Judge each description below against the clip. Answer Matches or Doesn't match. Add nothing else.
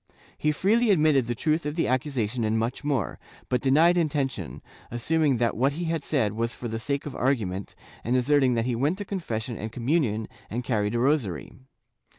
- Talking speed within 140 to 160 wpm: Doesn't match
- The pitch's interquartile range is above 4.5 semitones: Matches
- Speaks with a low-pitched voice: Matches